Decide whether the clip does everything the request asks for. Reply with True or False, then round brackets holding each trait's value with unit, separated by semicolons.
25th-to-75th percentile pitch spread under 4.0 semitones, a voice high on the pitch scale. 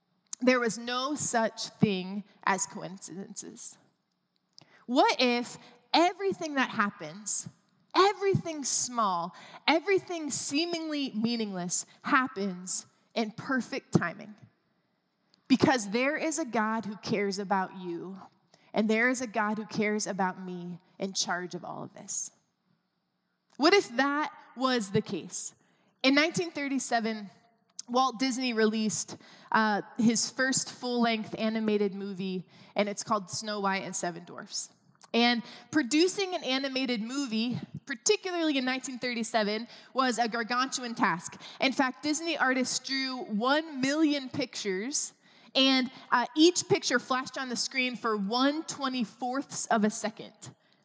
False (4.6 semitones; 235 Hz)